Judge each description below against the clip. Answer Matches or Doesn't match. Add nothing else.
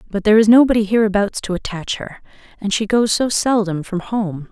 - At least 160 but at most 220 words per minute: Matches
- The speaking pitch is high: Matches